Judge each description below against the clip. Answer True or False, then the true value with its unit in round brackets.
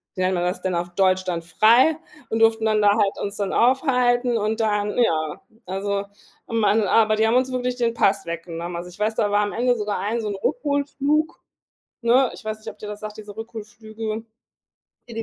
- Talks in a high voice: True (215 Hz)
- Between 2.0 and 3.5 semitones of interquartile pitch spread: True (2.8 semitones)